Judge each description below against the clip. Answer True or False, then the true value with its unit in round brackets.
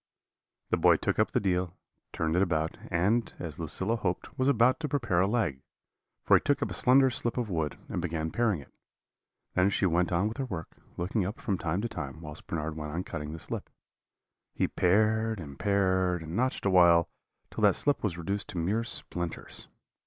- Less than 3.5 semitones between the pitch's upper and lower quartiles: False (5.1 semitones)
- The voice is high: False (90 Hz)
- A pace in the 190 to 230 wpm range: True (200 wpm)